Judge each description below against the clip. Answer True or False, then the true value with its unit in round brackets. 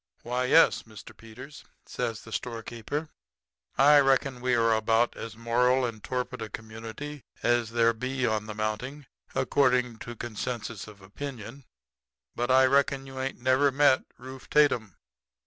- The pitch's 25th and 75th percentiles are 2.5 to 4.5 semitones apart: True (2.8 semitones)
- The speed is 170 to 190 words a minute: False (145 wpm)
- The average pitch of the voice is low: True (120 Hz)